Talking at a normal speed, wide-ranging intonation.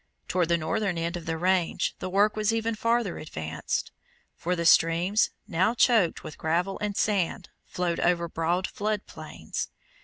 No: average, 160 wpm; average, 3.8 semitones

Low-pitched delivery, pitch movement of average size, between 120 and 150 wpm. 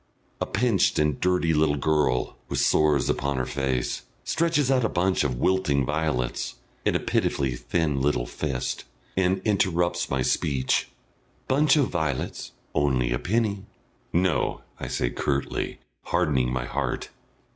No: very low, 75 Hz; wide, 5.9 semitones; average, 140 wpm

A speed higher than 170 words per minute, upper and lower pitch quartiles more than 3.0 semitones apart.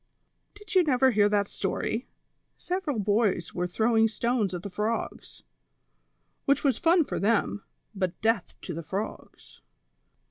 No: average, 140 wpm; average, 4.6 semitones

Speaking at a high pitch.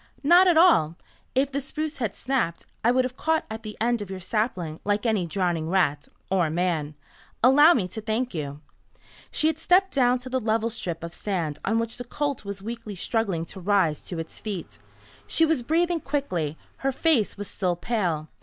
Yes: high, 220 Hz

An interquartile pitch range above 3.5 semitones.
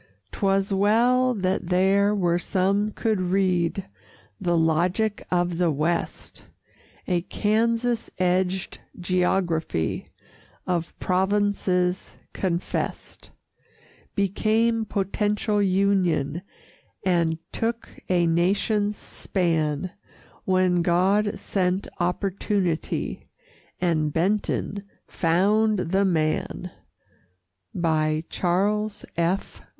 No: average, 2.9 semitones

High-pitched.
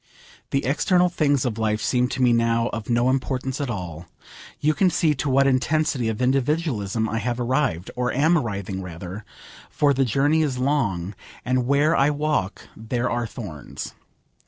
No: low, 125 Hz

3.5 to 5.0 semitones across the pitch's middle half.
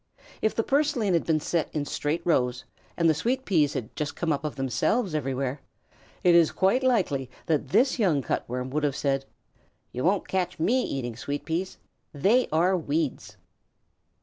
No: wide, 5.4 semitones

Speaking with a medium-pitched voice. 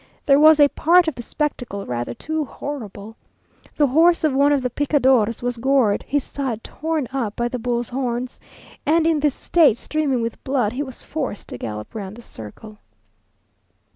No: very high, 260 Hz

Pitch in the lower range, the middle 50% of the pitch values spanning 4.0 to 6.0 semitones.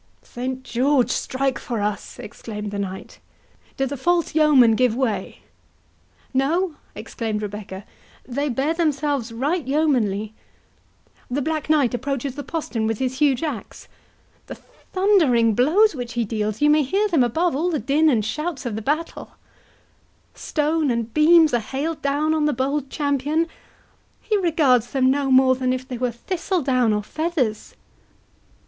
No: very high, 270 Hz; average, 4.5 semitones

